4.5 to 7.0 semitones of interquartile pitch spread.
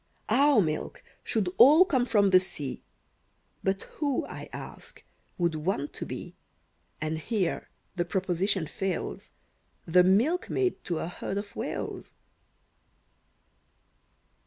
Yes: wide, 5.4 semitones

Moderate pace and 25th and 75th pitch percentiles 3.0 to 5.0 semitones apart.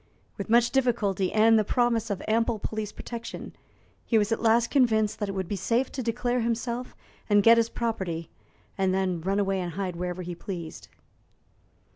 Yes: average, 180 wpm; average, 3.4 semitones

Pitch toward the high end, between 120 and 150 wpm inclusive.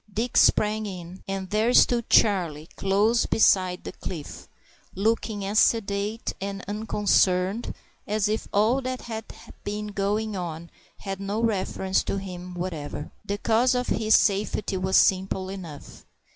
Yes: high, 200 Hz; average, 140 wpm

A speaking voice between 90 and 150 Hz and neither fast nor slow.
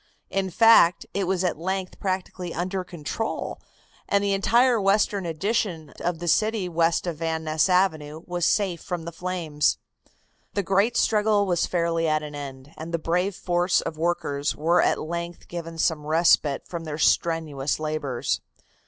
No: medium, 170 Hz; average, 160 wpm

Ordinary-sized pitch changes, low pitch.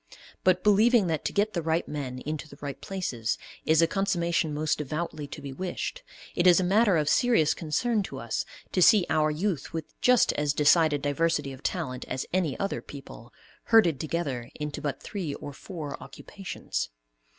No: average, 4.4 semitones; medium, 160 Hz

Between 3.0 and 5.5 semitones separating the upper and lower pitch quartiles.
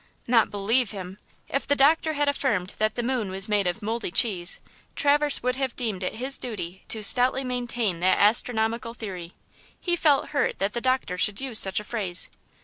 Yes: average, 4.7 semitones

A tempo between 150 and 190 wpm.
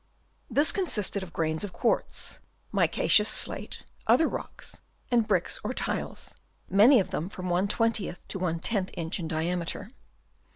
No: slow, 135 wpm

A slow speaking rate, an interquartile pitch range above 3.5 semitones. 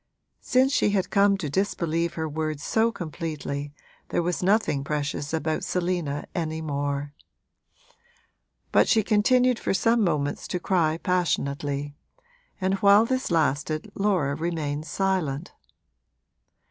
Yes: slow, 120 wpm; average, 4.9 semitones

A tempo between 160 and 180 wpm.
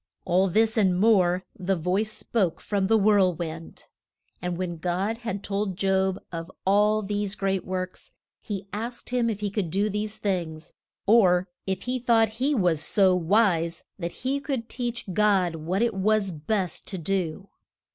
Yes: average, 165 wpm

